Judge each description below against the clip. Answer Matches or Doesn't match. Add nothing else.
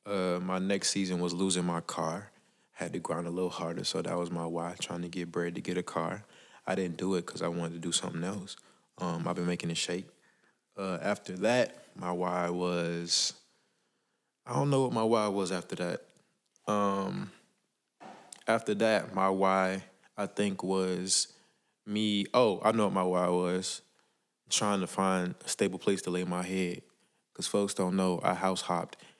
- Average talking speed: Matches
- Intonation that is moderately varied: Doesn't match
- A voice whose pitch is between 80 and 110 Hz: Matches